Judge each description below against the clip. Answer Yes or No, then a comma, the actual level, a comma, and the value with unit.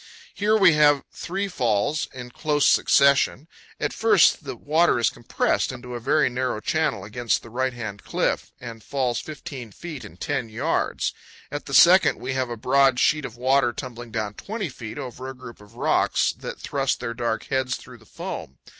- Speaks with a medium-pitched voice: No, low, 130 Hz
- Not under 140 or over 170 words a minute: No, average, 190 wpm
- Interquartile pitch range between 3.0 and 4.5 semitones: Yes, average, 3.7 semitones